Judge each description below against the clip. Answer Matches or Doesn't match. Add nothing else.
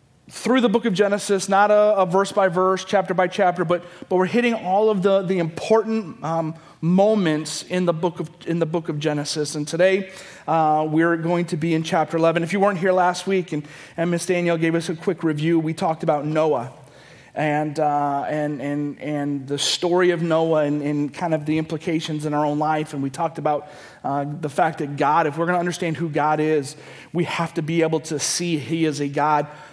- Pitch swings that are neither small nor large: Matches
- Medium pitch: Matches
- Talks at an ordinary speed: Doesn't match